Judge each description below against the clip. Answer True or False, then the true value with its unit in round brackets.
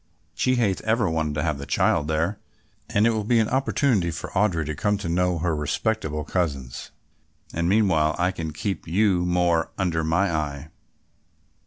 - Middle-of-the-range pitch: False (85 Hz)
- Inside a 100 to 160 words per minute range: False (175 wpm)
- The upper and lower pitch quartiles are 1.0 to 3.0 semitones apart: False (4.6 semitones)